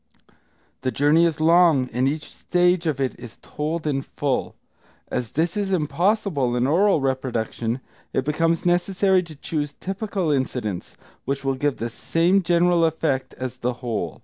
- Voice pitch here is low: No, medium, 150 Hz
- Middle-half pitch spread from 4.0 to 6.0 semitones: Yes, average, 5.0 semitones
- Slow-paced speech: No, average, 155 wpm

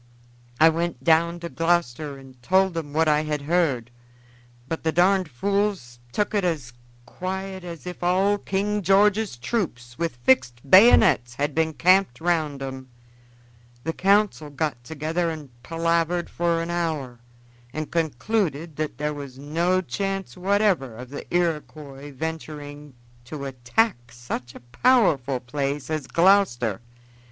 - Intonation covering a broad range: No, average, 4.9 semitones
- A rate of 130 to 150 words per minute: Yes, average, 140 wpm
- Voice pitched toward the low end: No, medium, 160 Hz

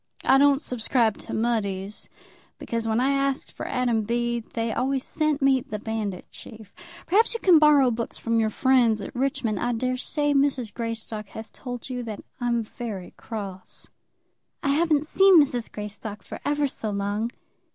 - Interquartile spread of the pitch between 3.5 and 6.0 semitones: Yes, average, 3.9 semitones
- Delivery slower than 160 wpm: No, average, 165 wpm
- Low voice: No, high, 240 Hz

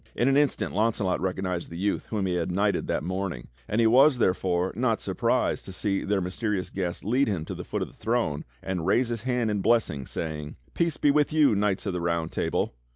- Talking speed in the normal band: No, fast, 220 wpm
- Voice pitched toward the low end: Yes, low, 100 Hz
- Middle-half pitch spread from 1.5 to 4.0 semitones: No, average, 4.5 semitones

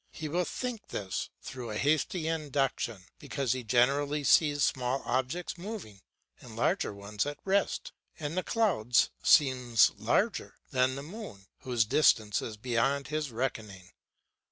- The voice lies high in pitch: No, low, 135 Hz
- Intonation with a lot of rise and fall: No, average, 5.0 semitones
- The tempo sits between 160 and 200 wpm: No, average, 140 wpm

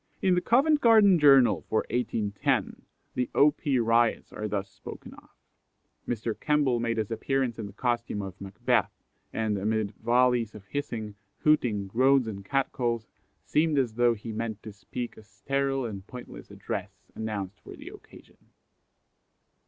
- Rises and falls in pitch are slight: No, average, 4.1 semitones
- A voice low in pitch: Yes, low, 115 Hz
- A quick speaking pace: No, average, 155 wpm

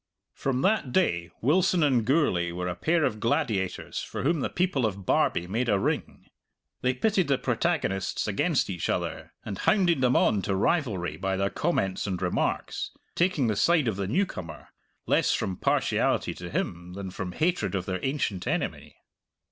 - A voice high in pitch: No, low, 115 Hz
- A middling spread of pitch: No, wide, 8.6 semitones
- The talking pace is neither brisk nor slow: Yes, average, 170 wpm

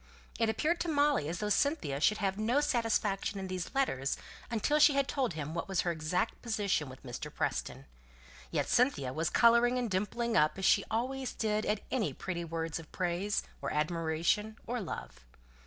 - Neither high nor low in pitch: No, high, 205 Hz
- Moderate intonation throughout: No, wide, 6.3 semitones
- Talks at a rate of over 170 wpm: Yes, average, 185 wpm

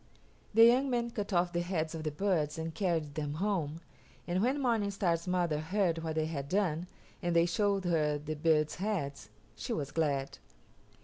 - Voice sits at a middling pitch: Yes, medium, 170 Hz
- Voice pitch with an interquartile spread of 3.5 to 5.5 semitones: Yes, average, 4.3 semitones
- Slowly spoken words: No, average, 185 wpm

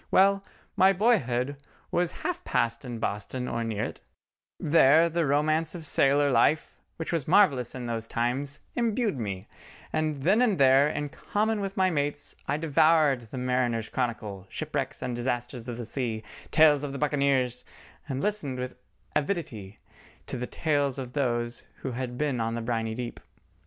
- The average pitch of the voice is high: No, low, 135 Hz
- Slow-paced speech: No, average, 165 wpm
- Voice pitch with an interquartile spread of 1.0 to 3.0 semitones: No, average, 4.5 semitones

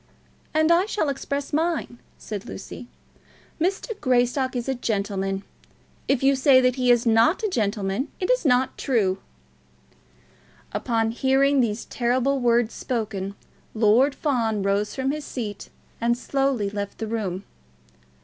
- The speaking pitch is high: Yes, high, 245 Hz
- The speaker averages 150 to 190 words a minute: No, average, 140 wpm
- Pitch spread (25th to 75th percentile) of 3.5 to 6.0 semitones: Yes, average, 4.3 semitones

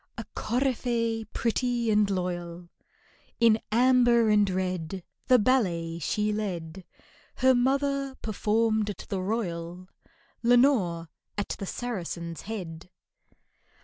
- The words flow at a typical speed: No, slow, 105 wpm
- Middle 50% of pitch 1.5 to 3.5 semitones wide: No, average, 5.0 semitones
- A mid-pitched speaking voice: No, high, 210 Hz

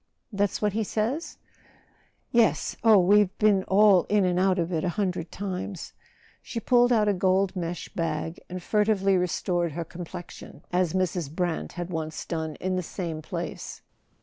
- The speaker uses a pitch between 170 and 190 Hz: Yes, medium, 185 Hz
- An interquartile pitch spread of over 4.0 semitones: No, average, 2.9 semitones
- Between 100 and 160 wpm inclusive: No, average, 175 wpm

